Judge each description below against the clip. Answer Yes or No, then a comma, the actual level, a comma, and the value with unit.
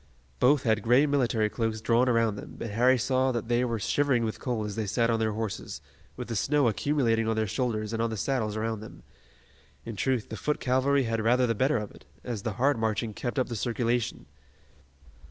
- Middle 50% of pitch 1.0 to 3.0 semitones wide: Yes, narrow, 2.5 semitones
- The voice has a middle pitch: No, low, 115 Hz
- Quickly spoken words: Yes, fast, 215 wpm